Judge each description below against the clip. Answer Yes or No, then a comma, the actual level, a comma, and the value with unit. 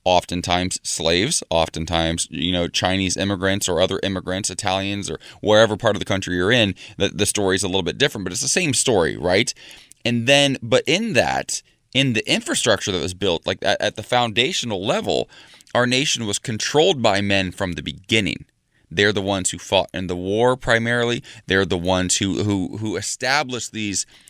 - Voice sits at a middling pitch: No, low, 100 Hz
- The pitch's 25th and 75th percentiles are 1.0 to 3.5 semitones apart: Yes, average, 3.2 semitones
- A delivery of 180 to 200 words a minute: Yes, average, 190 wpm